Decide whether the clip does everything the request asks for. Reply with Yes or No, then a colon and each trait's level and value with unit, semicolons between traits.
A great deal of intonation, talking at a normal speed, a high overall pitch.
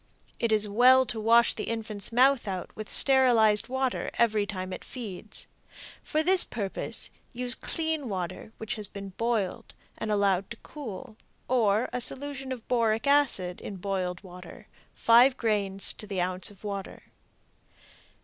No: average, 4.1 semitones; average, 150 wpm; high, 220 Hz